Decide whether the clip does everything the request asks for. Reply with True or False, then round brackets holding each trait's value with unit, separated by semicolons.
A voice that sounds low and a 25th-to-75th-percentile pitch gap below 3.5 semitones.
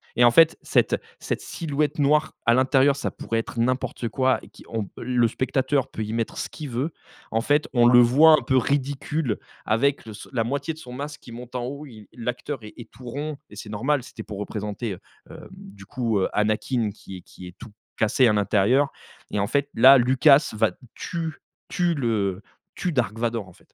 False (125 Hz; 4.1 semitones)